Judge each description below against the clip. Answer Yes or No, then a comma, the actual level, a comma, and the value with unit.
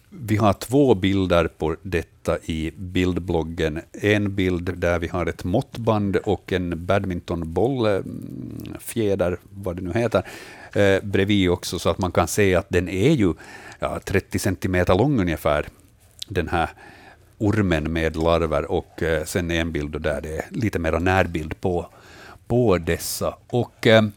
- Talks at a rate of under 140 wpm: No, average, 150 wpm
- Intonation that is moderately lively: Yes, average, 3.1 semitones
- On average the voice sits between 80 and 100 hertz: Yes, very low, 90 Hz